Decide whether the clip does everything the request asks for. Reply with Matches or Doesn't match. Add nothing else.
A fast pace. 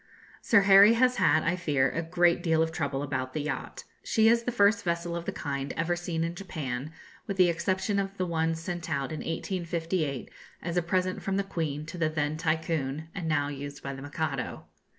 Matches